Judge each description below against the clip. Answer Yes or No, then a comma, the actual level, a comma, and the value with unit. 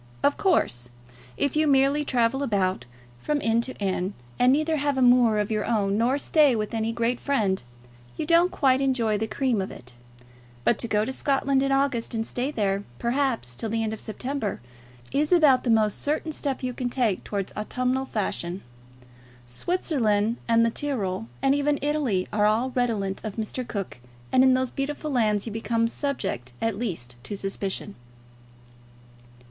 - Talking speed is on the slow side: No, average, 175 wpm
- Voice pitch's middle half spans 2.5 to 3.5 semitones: No, average, 4.6 semitones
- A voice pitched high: Yes, high, 235 Hz